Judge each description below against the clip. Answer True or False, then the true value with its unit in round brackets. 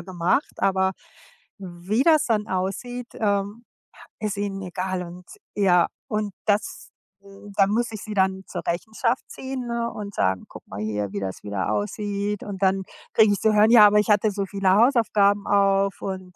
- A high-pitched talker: True (200 Hz)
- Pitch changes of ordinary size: False (2.3 semitones)